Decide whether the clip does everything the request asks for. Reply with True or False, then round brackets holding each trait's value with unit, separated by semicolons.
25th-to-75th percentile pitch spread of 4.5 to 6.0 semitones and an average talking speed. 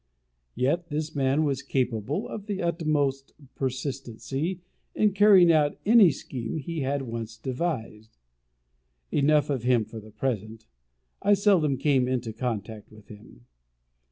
False (5.3 semitones; 130 wpm)